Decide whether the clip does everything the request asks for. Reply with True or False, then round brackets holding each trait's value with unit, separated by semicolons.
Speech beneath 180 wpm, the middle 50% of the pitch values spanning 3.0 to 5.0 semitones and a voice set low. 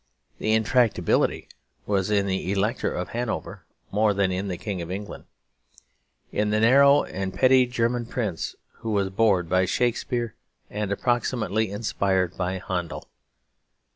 True (140 wpm; 3.5 semitones; 105 Hz)